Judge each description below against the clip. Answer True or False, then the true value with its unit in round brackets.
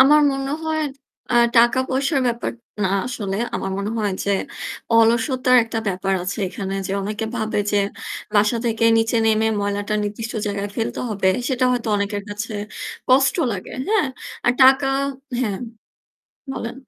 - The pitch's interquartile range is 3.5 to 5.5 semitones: True (3.8 semitones)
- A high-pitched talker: True (225 Hz)